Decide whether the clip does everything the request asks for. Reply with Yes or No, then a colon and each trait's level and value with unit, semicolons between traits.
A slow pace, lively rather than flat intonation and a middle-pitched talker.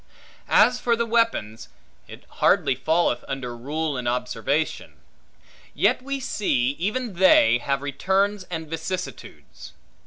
Yes: slow, 120 wpm; wide, 8.3 semitones; medium, 160 Hz